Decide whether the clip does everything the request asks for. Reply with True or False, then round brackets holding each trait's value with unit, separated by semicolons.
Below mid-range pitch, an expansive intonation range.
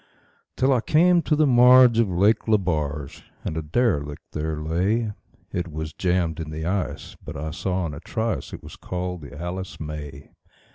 True (90 Hz; 6.5 semitones)